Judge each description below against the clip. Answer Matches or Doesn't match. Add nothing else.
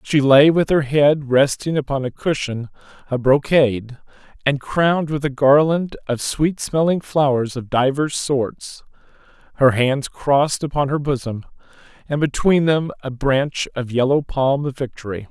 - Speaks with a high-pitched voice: Doesn't match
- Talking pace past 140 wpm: Matches